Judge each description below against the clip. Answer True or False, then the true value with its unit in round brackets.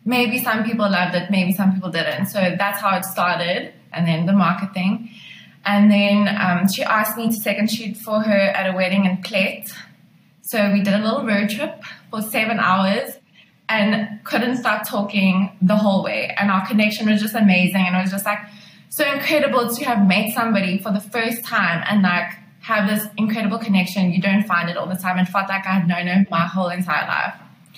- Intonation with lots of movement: False (2.4 semitones)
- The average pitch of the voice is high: True (200 Hz)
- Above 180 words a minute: True (205 wpm)